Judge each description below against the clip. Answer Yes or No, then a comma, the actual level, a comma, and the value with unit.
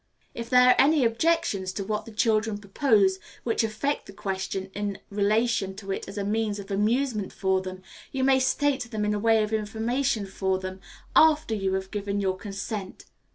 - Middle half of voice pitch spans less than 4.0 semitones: Yes, average, 3.1 semitones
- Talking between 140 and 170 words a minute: No, average, 190 wpm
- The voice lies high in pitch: Yes, high, 210 Hz